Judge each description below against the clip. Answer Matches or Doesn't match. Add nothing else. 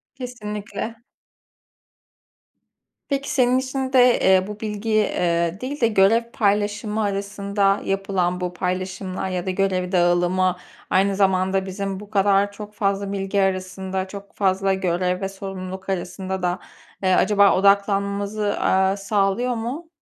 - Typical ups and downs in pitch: Doesn't match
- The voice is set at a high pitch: Matches